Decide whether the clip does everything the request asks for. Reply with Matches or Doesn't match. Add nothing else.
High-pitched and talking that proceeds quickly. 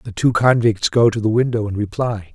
Doesn't match